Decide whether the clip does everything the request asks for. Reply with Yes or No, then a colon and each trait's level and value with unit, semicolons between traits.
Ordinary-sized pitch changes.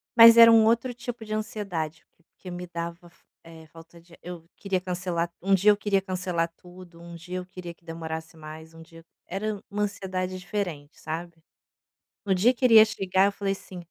Yes: average, 3.3 semitones